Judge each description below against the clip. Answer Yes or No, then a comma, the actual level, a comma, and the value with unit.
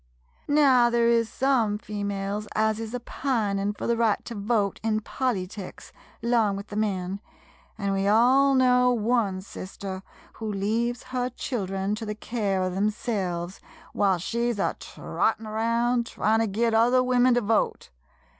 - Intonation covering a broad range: No, average, 3.1 semitones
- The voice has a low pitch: No, high, 220 Hz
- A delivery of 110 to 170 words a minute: Yes, average, 155 wpm